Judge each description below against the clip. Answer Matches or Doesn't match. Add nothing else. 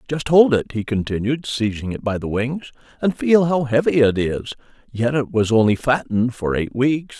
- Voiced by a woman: Doesn't match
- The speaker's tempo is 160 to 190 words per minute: Doesn't match